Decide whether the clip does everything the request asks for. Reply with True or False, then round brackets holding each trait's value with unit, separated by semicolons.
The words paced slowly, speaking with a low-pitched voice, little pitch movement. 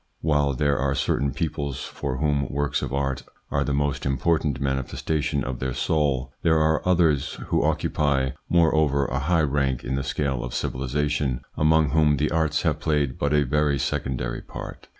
False (170 wpm; 70 Hz; 2.2 semitones)